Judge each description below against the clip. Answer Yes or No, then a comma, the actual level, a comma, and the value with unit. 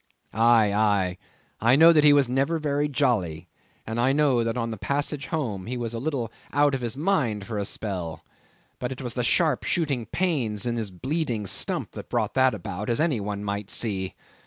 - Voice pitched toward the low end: Yes, low, 120 Hz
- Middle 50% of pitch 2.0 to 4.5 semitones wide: No, average, 5.3 semitones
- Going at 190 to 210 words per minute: Yes, fast, 205 wpm